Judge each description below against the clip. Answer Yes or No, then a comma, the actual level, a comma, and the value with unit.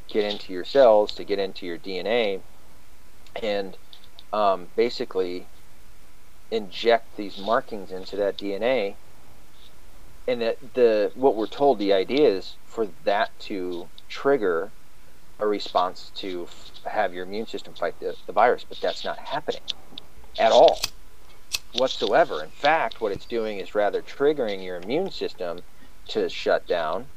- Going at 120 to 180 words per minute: Yes, average, 140 wpm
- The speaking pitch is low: Yes, low, 105 Hz